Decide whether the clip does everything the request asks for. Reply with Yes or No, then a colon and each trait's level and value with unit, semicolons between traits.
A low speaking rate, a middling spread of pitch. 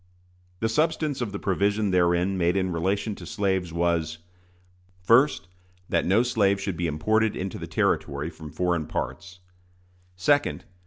No: average, 145 wpm; average, 3.7 semitones